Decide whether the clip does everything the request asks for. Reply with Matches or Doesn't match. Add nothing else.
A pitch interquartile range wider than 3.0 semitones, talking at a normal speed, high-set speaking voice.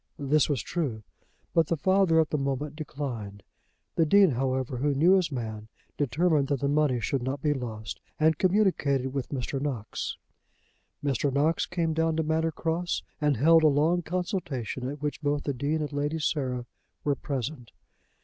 Doesn't match